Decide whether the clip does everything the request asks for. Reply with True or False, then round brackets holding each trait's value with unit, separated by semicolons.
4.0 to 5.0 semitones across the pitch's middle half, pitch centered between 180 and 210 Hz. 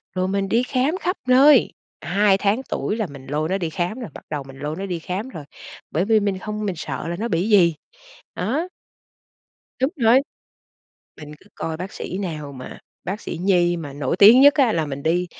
False (5.6 semitones; 190 Hz)